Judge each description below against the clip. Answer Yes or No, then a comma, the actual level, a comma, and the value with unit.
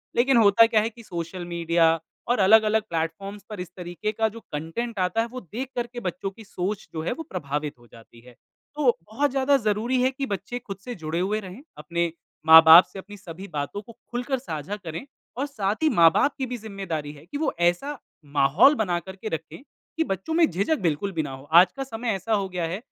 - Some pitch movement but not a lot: No, wide, 5.7 semitones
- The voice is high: Yes, high, 200 Hz